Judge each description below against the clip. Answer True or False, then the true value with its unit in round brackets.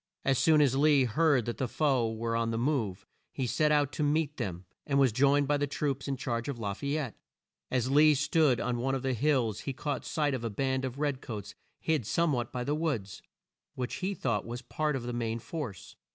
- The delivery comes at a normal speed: False (235 wpm)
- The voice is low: True (130 Hz)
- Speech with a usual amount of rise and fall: True (3.7 semitones)